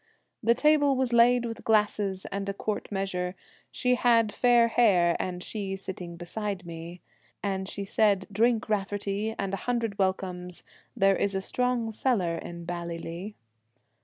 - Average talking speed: Yes, average, 150 wpm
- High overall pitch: Yes, high, 200 Hz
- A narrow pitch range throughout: No, average, 3.8 semitones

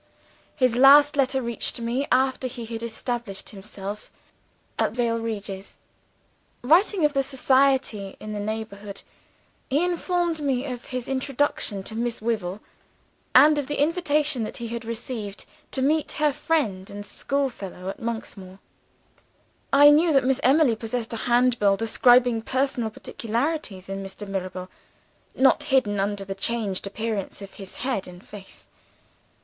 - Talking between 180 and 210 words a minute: No, average, 145 wpm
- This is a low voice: No, high, 235 Hz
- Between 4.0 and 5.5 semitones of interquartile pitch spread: Yes, average, 4.9 semitones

